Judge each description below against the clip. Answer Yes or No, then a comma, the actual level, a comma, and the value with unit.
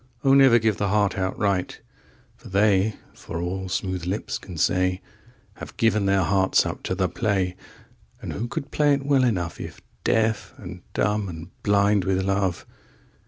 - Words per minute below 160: Yes, average, 150 wpm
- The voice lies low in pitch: Yes, low, 100 Hz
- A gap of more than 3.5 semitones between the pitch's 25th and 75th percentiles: No, average, 2.7 semitones